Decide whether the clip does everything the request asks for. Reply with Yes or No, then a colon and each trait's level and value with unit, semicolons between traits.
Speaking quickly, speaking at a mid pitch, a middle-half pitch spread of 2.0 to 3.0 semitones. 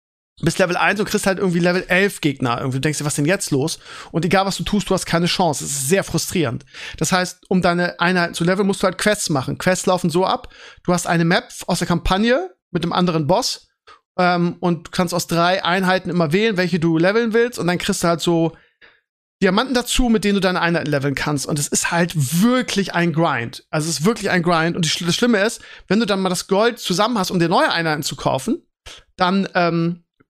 Yes: fast, 235 wpm; medium, 180 Hz; narrow, 2.5 semitones